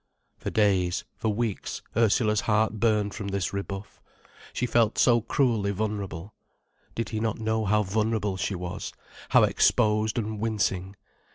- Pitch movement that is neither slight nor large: No, narrow, 1.9 semitones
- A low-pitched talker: Yes, low, 105 Hz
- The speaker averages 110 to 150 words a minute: Yes, average, 145 wpm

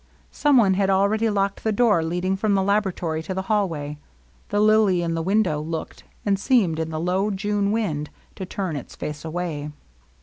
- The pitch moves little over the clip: No, average, 4.1 semitones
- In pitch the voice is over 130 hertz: Yes, high, 190 Hz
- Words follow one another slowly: No, average, 190 wpm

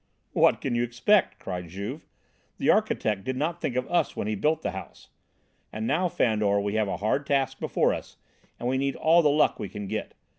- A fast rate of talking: Yes, fast, 215 wpm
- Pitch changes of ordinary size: No, wide, 6.0 semitones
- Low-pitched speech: Yes, low, 120 Hz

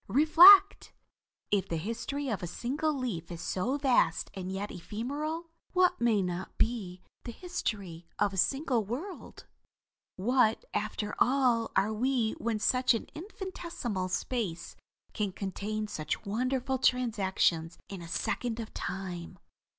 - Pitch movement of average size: No, wide, 5.7 semitones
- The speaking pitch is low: No, high, 225 Hz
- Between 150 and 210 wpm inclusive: No, slow, 135 wpm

